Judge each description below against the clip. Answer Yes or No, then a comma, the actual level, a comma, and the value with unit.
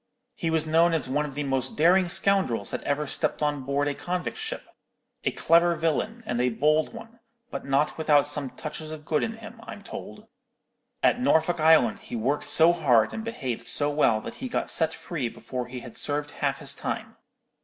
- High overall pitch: No, medium, 150 Hz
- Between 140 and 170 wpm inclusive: No, average, 200 wpm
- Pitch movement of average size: Yes, average, 3.8 semitones